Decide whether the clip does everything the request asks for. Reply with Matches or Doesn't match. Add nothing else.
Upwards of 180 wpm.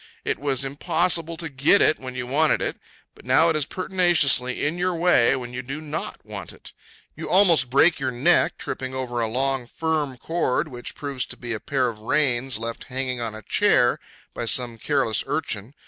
Matches